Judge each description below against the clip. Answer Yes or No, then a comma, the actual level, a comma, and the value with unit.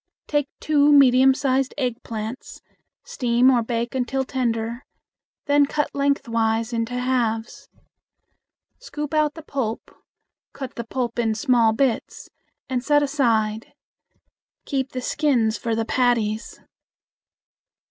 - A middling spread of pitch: Yes, average, 3.3 semitones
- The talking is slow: Yes, slow, 115 wpm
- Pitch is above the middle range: Yes, very high, 250 Hz